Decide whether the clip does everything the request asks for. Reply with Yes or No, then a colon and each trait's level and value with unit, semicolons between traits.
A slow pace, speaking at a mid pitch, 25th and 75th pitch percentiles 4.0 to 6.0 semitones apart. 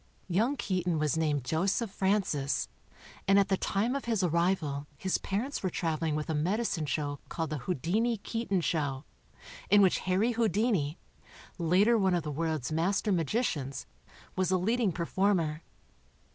No: average, 160 wpm; medium, 180 Hz; average, 4.6 semitones